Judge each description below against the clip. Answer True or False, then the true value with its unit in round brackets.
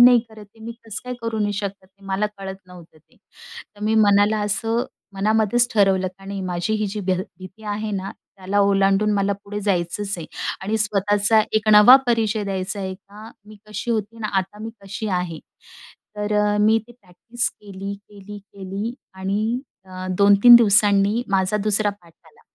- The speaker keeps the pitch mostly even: True (1.9 semitones)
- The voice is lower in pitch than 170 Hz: False (205 Hz)